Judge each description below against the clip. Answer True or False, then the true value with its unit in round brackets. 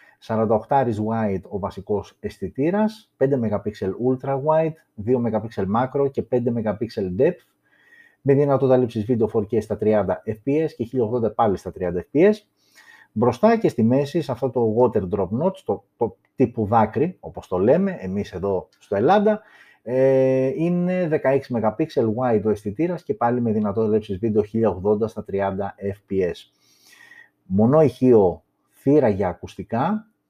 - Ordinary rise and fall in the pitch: True (4.9 semitones)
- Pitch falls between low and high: False (120 Hz)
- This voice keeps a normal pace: True (145 wpm)